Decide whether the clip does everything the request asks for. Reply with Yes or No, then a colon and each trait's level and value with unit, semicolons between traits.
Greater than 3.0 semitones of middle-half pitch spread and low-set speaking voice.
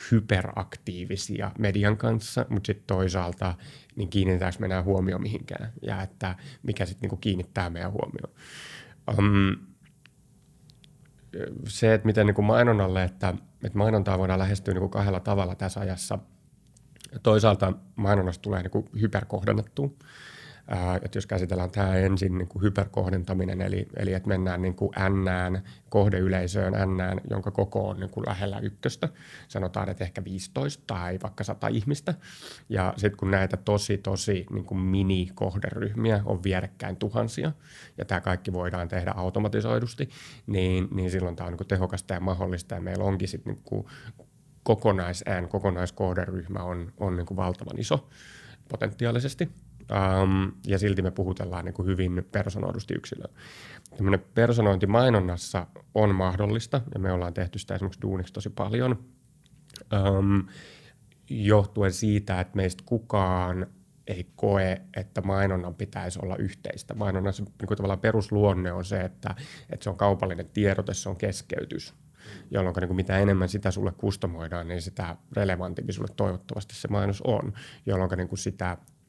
No: narrow, 2.6 semitones; low, 100 Hz